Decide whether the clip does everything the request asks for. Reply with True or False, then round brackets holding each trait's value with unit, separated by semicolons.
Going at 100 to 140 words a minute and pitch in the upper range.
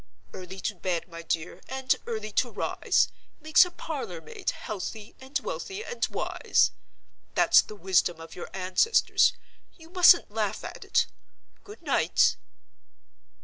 True (135 wpm; 215 Hz)